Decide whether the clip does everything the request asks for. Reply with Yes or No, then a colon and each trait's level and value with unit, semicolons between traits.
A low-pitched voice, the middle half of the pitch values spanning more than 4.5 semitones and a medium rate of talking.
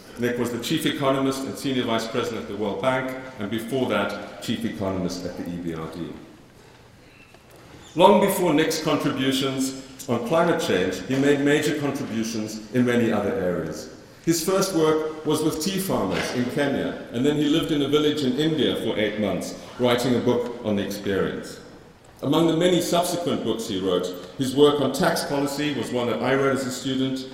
Yes: low, 130 Hz; average, 5.1 semitones; average, 180 wpm